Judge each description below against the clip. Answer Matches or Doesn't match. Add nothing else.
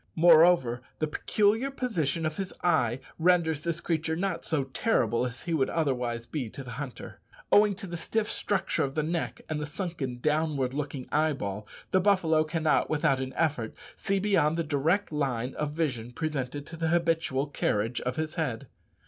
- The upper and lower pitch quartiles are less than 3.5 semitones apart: Doesn't match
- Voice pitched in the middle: Matches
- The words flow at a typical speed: Matches